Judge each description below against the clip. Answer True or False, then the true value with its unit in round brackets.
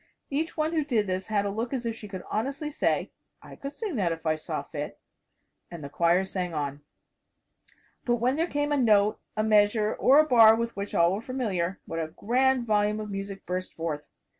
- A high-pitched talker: True (215 Hz)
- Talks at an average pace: False (215 wpm)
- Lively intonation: True (5.7 semitones)